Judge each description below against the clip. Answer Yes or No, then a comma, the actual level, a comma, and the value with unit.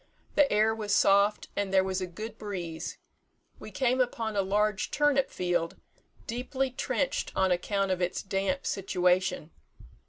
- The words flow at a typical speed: Yes, average, 150 wpm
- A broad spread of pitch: No, average, 3.2 semitones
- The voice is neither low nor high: No, high, 200 Hz